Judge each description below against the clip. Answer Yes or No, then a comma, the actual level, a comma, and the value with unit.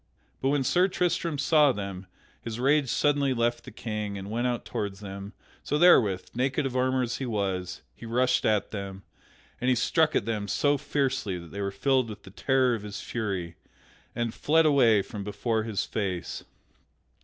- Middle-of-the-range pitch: No, low, 115 Hz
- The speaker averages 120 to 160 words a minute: No, average, 185 wpm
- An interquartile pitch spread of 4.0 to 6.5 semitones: Yes, average, 5.0 semitones